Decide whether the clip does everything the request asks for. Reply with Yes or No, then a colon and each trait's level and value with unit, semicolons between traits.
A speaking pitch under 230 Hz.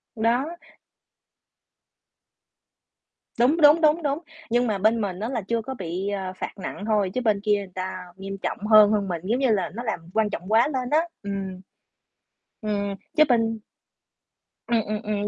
Yes: high, 215 Hz